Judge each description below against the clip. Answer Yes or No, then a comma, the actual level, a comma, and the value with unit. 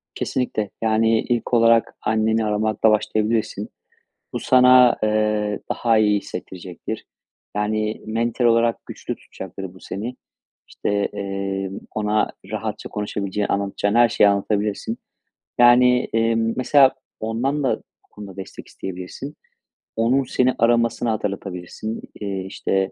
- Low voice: Yes, low, 110 Hz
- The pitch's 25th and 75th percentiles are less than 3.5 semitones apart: Yes, narrow, 2.4 semitones